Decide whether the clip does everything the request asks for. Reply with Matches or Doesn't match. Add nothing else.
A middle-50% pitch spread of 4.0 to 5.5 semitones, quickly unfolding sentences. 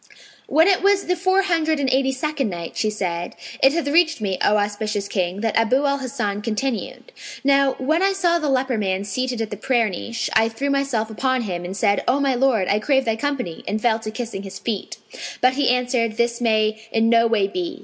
Matches